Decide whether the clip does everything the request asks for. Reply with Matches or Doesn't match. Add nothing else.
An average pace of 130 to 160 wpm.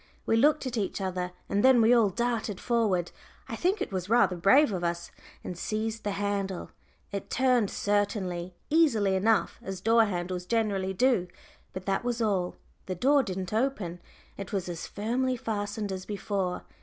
Doesn't match